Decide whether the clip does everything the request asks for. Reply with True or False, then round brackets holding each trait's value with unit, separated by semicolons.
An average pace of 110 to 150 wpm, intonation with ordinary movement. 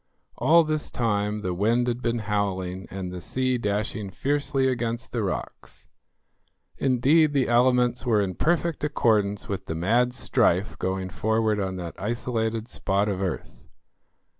True (145 wpm; 4.2 semitones)